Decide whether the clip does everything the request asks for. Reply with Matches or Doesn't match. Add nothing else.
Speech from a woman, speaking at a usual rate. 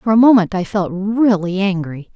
Matches